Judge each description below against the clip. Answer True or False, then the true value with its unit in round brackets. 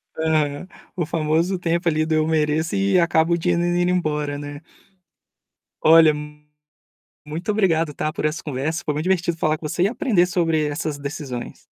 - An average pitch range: False (2.3 semitones)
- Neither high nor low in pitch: True (160 Hz)